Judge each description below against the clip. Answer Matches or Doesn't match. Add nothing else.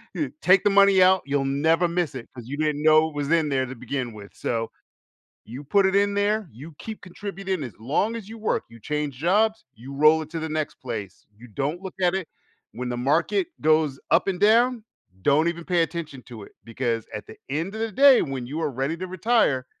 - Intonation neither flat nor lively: Doesn't match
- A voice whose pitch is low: Doesn't match